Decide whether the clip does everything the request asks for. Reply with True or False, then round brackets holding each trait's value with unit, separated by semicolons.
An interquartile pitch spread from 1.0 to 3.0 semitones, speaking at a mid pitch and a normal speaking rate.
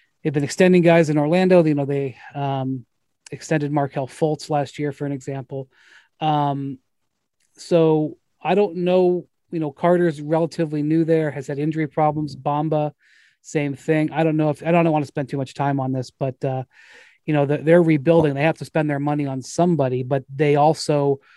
True (2.5 semitones; 150 Hz; 190 wpm)